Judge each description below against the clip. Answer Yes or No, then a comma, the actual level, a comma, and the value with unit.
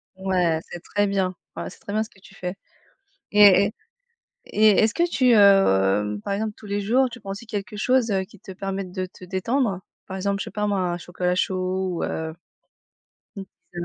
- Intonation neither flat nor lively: No, narrow, 2.3 semitones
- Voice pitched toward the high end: Yes, high, 195 Hz